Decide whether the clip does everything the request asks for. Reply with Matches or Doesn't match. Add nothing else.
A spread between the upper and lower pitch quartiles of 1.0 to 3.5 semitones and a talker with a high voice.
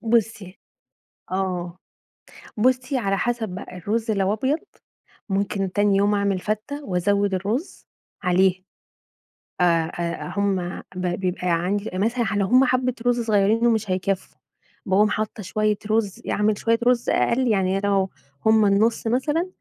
Matches